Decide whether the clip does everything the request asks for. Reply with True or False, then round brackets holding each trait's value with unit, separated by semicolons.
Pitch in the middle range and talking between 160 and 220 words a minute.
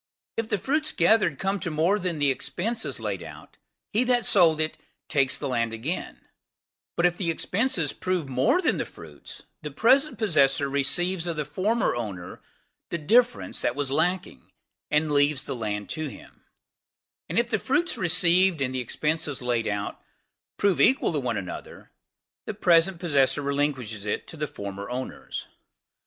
True (160 Hz; 165 wpm)